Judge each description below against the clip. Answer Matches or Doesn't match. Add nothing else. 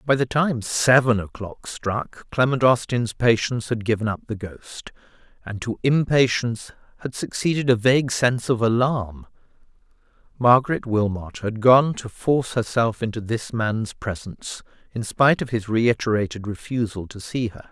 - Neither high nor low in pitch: Doesn't match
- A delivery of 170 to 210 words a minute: Doesn't match